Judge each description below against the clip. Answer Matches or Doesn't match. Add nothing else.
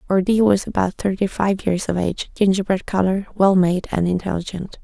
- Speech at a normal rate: Matches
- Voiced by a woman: Matches